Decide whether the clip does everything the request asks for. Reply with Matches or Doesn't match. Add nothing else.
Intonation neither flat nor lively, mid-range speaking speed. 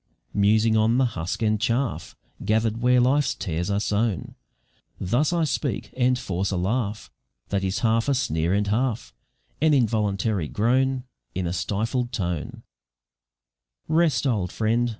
Matches